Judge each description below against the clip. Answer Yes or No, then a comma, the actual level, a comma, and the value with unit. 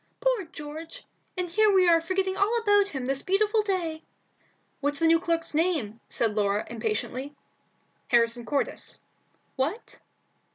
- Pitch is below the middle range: No, very high, 330 Hz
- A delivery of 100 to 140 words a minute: Yes, slow, 135 wpm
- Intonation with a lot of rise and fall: Yes, wide, 6.3 semitones